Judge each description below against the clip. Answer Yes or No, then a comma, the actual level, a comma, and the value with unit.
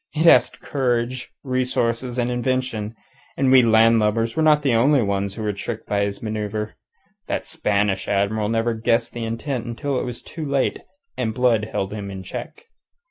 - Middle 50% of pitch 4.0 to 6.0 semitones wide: No, average, 3.3 semitones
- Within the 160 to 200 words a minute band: Yes, average, 175 wpm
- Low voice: Yes, low, 115 Hz